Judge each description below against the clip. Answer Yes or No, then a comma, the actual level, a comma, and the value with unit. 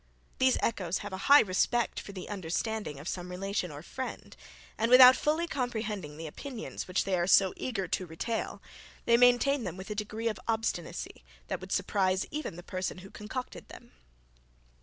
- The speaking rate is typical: Yes, average, 180 wpm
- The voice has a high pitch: Yes, high, 205 Hz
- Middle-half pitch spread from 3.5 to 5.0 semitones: Yes, average, 4.7 semitones